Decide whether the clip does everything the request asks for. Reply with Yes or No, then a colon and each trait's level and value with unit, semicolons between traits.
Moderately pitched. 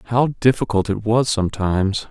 No: low, 110 Hz